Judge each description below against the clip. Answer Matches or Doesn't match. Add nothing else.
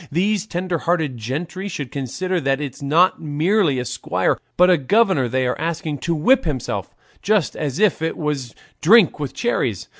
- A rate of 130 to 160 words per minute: Doesn't match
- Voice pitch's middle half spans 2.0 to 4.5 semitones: Doesn't match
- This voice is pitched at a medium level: Matches